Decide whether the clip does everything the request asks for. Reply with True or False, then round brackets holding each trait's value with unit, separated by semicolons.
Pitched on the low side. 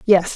False (190 Hz)